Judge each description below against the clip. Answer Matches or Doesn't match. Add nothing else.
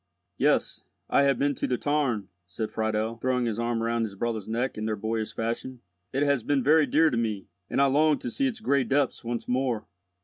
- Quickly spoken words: Matches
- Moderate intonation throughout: Matches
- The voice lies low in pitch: Matches